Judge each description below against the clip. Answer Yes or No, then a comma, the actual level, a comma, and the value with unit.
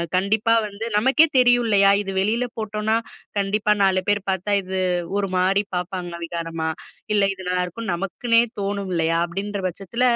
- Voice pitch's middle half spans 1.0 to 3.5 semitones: Yes, average, 2.8 semitones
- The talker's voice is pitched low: No, high, 200 Hz